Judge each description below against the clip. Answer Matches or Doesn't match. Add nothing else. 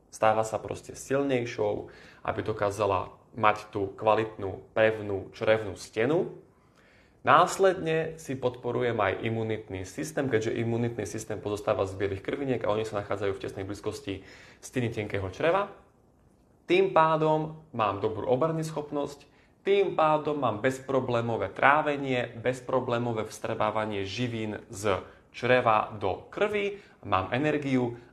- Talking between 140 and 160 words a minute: Doesn't match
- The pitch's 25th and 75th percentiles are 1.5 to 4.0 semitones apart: Doesn't match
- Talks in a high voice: Doesn't match